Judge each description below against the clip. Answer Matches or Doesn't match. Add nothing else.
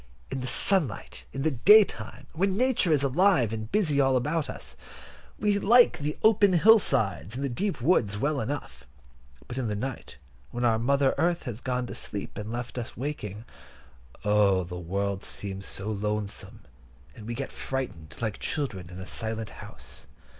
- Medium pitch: Doesn't match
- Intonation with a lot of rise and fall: Matches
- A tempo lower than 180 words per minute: Matches